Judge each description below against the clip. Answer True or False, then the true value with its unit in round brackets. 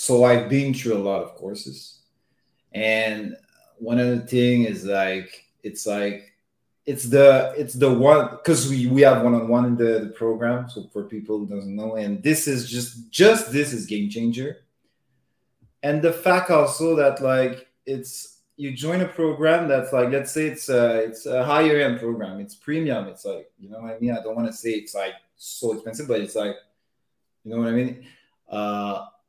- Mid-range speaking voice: False (125 Hz)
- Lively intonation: False (4.5 semitones)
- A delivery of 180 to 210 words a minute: True (195 wpm)